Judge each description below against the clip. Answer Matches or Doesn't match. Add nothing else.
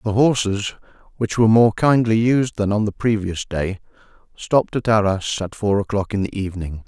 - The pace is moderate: Matches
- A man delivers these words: Matches